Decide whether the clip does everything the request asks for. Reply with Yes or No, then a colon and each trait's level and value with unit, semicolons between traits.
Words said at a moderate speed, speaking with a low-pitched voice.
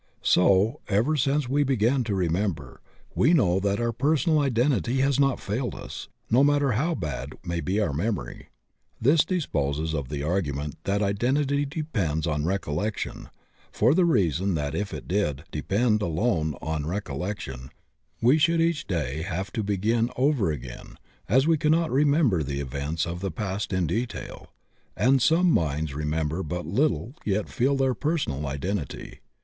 Yes: average, 160 wpm; low, 100 Hz